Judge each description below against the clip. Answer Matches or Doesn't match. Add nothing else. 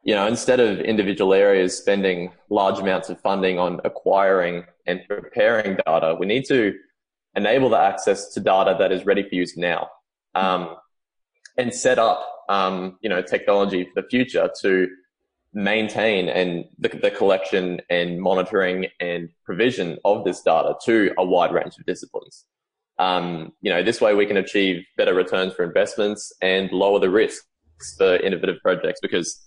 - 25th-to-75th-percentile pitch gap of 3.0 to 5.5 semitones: Doesn't match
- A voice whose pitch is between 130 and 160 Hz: Doesn't match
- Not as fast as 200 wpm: Matches